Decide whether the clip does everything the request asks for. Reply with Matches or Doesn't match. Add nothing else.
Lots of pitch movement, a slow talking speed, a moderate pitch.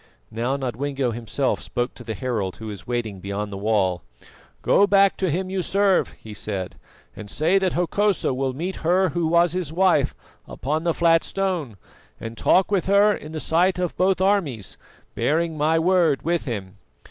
Doesn't match